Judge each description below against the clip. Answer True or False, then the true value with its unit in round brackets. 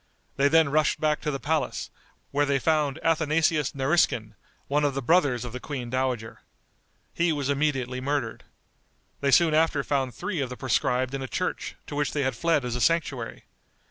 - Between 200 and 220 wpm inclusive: False (185 wpm)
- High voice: False (140 Hz)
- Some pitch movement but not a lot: True (3.1 semitones)